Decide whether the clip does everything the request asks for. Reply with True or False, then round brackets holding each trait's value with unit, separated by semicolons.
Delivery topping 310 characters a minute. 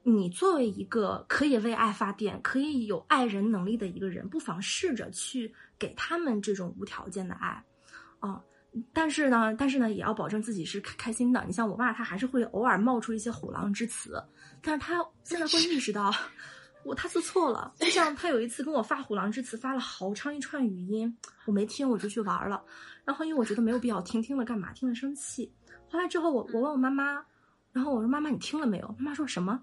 True (330 characters per minute)